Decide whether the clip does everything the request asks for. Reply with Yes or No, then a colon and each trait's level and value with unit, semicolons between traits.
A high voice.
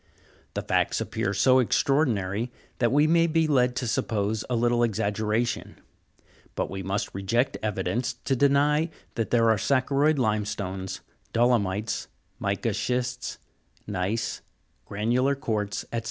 No: low, 115 Hz